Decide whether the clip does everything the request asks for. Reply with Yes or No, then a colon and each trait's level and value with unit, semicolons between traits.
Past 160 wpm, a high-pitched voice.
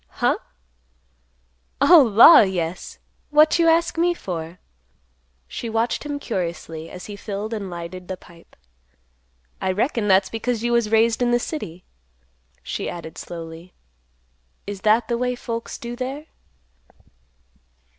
No: slow, 135 wpm; high, 220 Hz